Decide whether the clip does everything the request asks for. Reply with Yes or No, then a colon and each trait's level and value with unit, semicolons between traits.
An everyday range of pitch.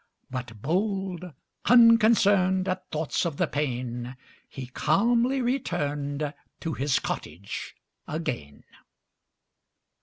No: wide, 6.9 semitones